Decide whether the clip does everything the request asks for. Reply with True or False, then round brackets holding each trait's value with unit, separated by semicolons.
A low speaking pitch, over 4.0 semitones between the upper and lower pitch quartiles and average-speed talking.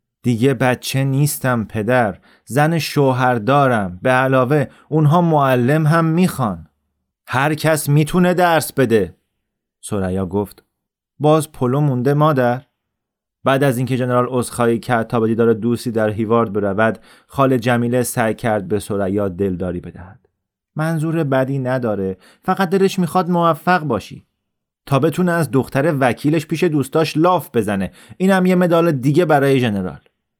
True (130 Hz; 5.4 semitones; 130 wpm)